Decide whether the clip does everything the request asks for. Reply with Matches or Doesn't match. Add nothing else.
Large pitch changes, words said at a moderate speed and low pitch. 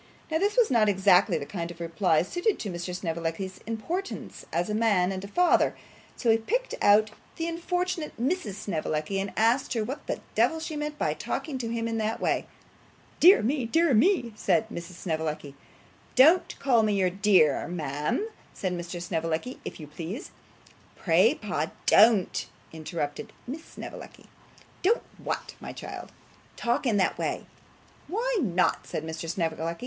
Doesn't match